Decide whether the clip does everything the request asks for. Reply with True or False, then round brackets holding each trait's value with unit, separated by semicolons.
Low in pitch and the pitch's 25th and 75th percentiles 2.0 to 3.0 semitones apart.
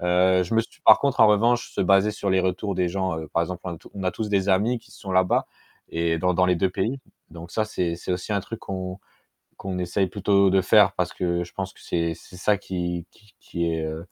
True (95 Hz; 2.4 semitones)